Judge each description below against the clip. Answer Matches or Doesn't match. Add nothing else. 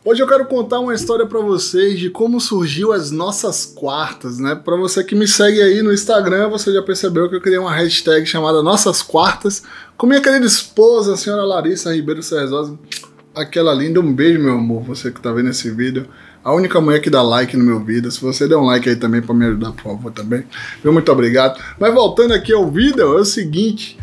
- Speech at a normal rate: Doesn't match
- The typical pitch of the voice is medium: Matches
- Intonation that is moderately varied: Doesn't match